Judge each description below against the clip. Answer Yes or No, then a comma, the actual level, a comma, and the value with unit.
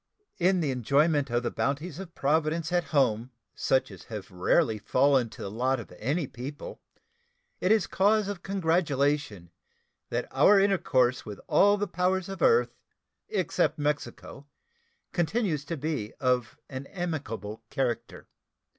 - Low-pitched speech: No, medium, 145 Hz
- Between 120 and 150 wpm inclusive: Yes, average, 145 wpm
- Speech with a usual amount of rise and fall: No, wide, 6.0 semitones